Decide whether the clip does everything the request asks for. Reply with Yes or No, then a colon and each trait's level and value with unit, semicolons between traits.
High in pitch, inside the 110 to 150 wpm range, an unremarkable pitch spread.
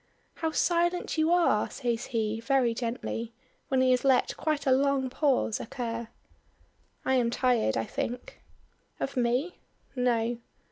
Yes: very high, 250 Hz; average, 140 wpm; average, 3.0 semitones